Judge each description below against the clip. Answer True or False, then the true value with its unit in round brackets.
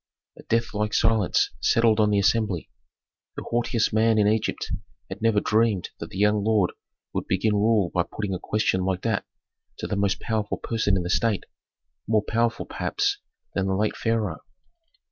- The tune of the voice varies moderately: False (2.3 semitones)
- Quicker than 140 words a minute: True (170 wpm)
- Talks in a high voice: False (105 Hz)